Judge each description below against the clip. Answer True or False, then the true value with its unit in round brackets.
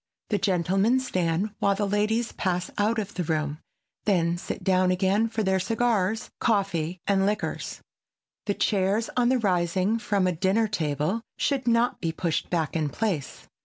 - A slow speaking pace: False (160 wpm)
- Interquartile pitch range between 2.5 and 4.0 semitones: True (3.7 semitones)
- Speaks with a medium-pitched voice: False (195 Hz)